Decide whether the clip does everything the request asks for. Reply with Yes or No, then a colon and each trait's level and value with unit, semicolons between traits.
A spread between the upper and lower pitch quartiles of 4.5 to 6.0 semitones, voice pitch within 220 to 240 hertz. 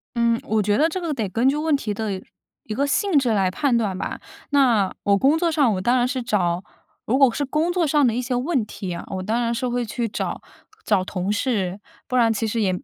Yes: average, 5.0 semitones; high, 235 Hz